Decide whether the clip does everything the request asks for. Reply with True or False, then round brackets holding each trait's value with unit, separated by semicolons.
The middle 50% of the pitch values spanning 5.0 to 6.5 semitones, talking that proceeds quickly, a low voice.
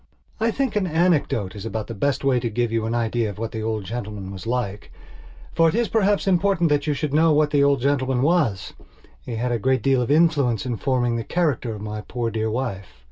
True (5.4 semitones; 235 wpm; 125 Hz)